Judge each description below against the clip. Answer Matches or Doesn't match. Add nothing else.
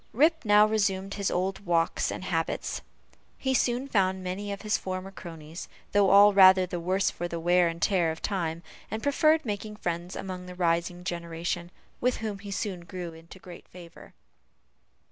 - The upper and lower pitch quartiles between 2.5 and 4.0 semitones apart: Matches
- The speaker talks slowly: Doesn't match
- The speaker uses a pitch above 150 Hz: Matches